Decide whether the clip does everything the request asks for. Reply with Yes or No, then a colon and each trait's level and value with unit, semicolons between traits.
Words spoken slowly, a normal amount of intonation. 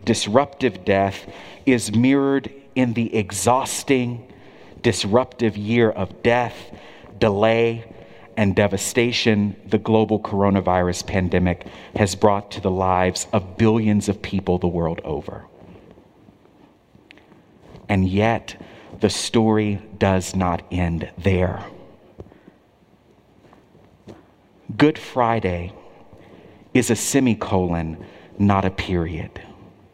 Yes: slow, 90 wpm; average, 3.5 semitones